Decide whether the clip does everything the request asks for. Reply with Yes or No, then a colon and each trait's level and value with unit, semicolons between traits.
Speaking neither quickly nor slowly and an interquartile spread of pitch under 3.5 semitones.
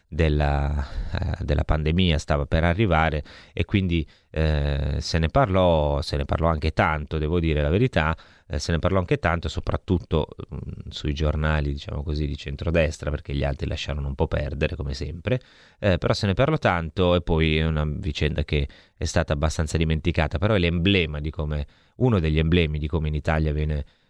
No: fast, 185 wpm; average, 3.0 semitones